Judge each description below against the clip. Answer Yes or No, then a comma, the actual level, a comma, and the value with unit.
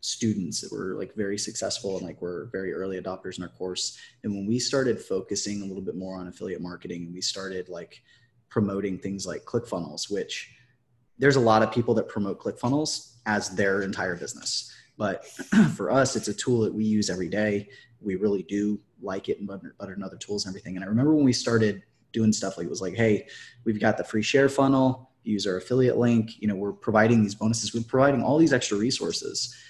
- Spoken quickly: Yes, fast, 215 wpm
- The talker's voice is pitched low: Yes, low, 110 Hz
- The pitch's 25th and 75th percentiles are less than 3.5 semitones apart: No, average, 3.8 semitones